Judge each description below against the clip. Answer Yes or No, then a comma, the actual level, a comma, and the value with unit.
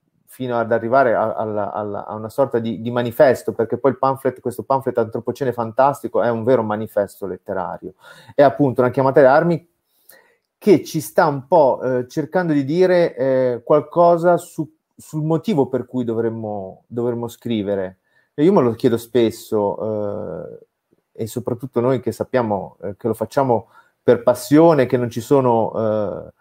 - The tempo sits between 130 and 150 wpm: No, average, 165 wpm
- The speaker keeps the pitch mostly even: No, average, 3.8 semitones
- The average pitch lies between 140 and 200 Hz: No, low, 125 Hz